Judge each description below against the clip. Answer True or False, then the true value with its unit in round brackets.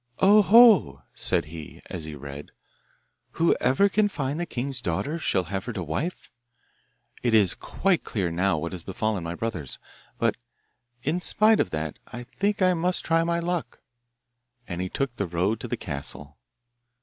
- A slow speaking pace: False (165 wpm)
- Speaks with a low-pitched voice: True (115 Hz)